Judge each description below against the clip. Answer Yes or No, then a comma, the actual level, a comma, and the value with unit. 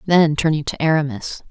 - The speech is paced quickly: No, average, 160 wpm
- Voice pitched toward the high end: No, medium, 150 Hz